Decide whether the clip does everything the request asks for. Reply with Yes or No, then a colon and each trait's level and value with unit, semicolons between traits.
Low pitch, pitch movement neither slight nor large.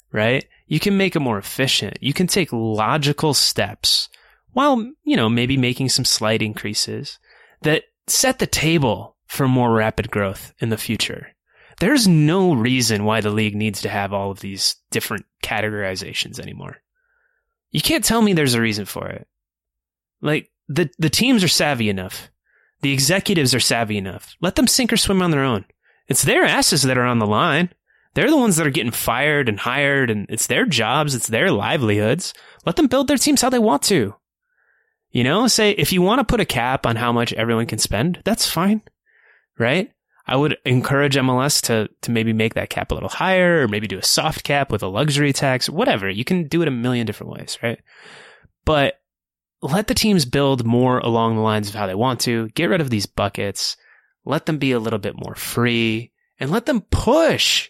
No: low, 130 Hz; wide, 8.0 semitones